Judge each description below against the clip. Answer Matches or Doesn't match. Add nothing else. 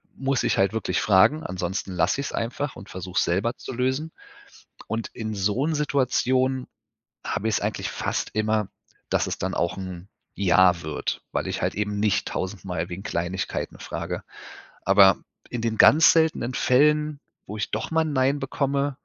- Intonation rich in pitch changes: Matches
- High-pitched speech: Doesn't match